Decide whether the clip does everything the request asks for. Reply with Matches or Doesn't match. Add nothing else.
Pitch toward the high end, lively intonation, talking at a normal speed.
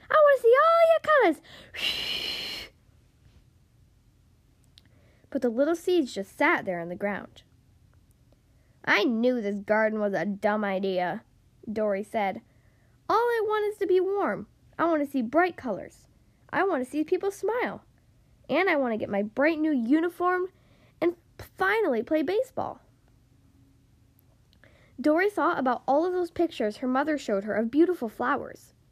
Matches